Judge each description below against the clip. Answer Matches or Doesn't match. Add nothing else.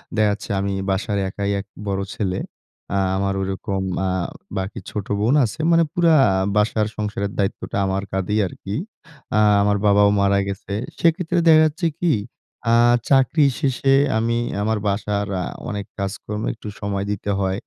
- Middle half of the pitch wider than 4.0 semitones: Doesn't match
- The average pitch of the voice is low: Matches